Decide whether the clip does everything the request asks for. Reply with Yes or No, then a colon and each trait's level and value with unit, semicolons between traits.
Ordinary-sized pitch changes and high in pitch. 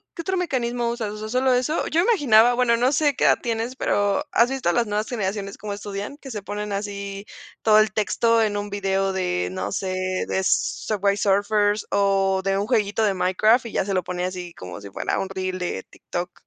Yes: average, 3.3 semitones; high, 205 Hz